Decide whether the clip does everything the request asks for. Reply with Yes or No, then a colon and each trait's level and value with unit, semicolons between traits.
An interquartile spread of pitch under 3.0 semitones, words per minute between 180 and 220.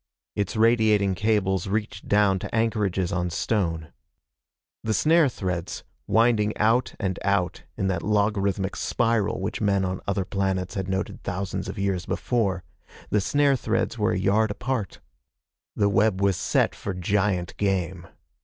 No: narrow, 2.5 semitones; average, 145 wpm